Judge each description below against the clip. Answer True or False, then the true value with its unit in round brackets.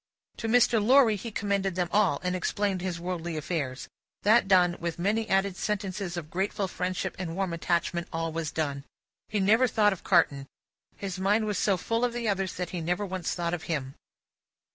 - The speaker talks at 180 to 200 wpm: True (190 wpm)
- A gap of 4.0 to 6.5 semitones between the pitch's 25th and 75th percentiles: False (3.2 semitones)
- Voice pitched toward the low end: False (185 Hz)